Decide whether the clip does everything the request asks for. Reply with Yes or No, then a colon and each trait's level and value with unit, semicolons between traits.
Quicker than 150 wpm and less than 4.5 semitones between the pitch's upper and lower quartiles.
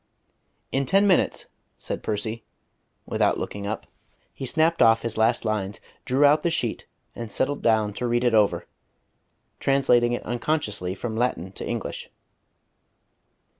No: average, 140 wpm; average, 4.0 semitones